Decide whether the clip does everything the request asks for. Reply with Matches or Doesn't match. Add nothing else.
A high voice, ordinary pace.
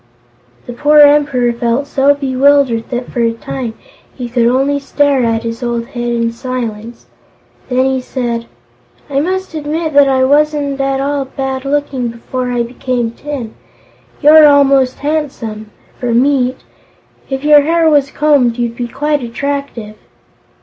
Matches